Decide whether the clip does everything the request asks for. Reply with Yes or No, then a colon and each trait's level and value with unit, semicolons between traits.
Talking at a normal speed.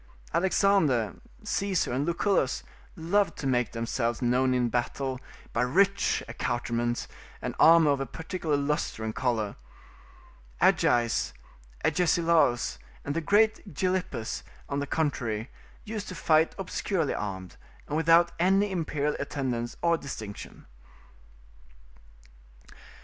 No: slow, 115 wpm